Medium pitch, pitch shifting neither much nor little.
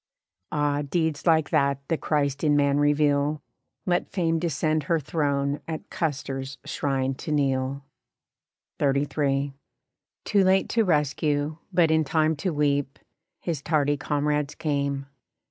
No: medium, 145 Hz; narrow, 2.1 semitones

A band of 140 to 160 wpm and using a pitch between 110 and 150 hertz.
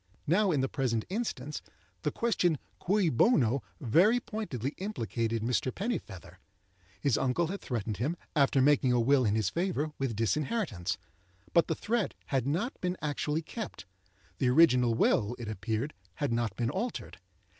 Yes: average, 155 wpm; medium, 140 Hz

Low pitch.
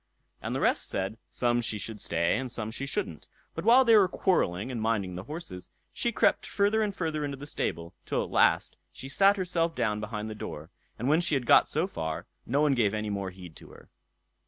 Yes: low, 120 Hz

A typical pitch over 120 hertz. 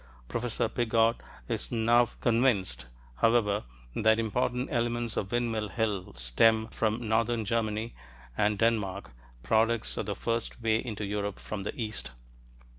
No: low, 110 Hz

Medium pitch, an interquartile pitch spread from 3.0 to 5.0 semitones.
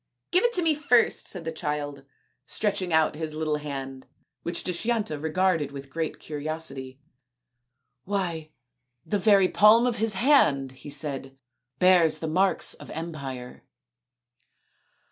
No: medium, 160 Hz; wide, 5.4 semitones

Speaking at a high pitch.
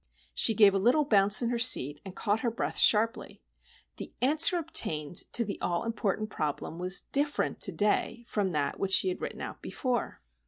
Yes: high, 210 Hz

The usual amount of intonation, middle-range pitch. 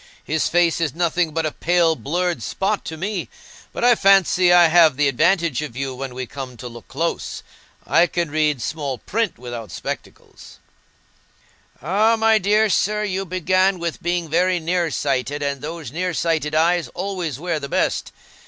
Yes: average, 3.9 semitones; medium, 170 Hz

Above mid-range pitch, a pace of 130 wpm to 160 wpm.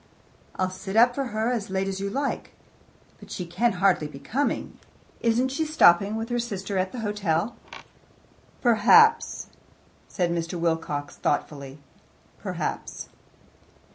Yes: high, 200 Hz; slow, 135 wpm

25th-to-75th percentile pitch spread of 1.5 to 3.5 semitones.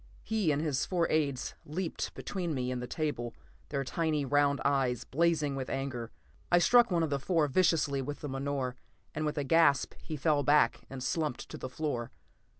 Yes: average, 3.1 semitones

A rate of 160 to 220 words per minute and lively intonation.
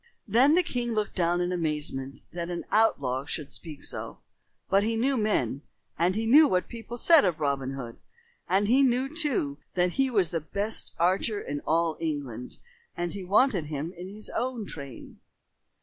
Yes: average, 180 wpm; wide, 6.8 semitones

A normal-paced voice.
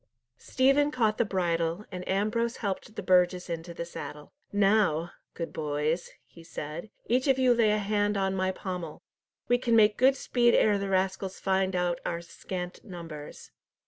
Yes: average, 170 wpm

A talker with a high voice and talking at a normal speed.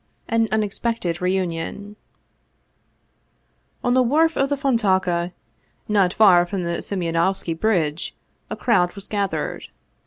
No: high, 195 Hz; slow, 115 wpm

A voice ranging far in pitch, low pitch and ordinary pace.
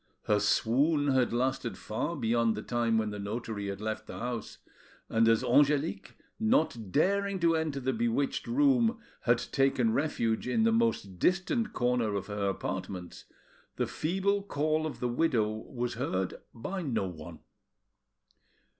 Yes: wide, 6.3 semitones; low, 125 Hz; average, 150 wpm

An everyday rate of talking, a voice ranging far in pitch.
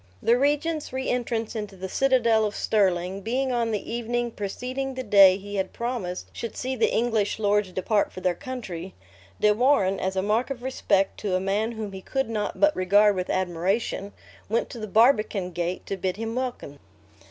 No: average, 190 wpm; average, 4.0 semitones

